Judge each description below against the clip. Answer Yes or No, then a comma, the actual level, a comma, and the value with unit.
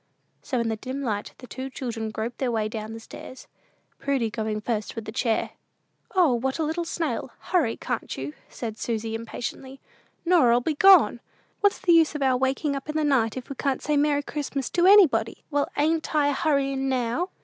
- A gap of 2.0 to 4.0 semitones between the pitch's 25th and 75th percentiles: No, average, 4.7 semitones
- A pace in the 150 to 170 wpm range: No, average, 195 wpm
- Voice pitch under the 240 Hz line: No, very high, 265 Hz